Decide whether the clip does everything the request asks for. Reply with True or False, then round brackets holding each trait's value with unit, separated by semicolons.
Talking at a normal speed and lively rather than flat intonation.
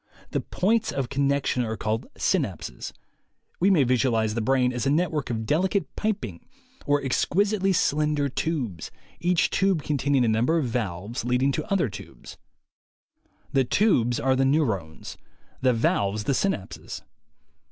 True (145 wpm; 6.1 semitones)